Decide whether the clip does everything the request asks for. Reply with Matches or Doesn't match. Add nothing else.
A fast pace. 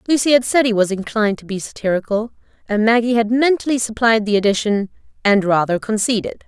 Doesn't match